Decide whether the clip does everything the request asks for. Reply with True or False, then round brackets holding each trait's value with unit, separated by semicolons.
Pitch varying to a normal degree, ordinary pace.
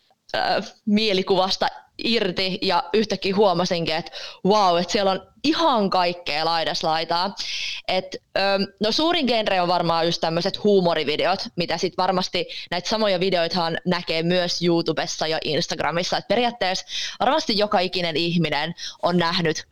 True (3.4 semitones; 135 wpm)